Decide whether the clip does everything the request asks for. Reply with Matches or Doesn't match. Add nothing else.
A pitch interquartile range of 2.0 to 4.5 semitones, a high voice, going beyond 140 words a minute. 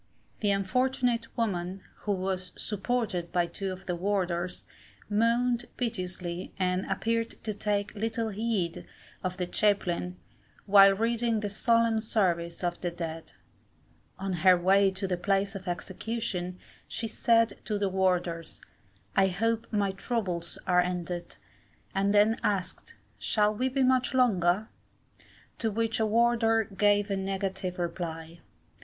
Doesn't match